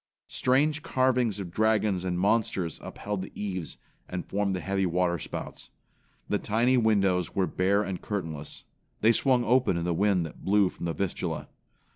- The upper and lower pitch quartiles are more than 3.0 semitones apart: Yes, average, 3.5 semitones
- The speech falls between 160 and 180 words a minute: Yes, average, 165 wpm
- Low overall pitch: Yes, low, 100 Hz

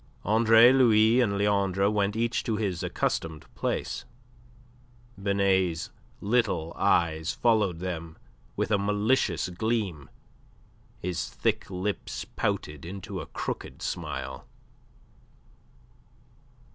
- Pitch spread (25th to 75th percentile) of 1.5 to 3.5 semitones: No, average, 4.1 semitones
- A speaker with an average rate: No, slow, 95 wpm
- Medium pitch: No, low, 100 Hz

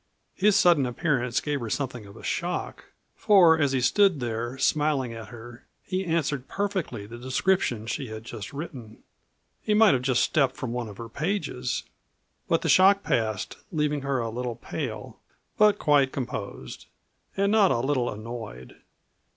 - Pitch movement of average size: No, wide, 6.1 semitones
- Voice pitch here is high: No, low, 130 Hz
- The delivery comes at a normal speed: Yes, average, 165 wpm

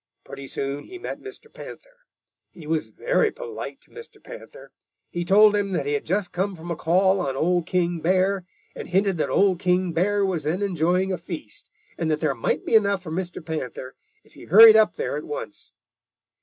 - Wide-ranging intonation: No, average, 4.0 semitones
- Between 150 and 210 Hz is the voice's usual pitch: Yes, medium, 185 Hz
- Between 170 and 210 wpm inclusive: Yes, average, 200 wpm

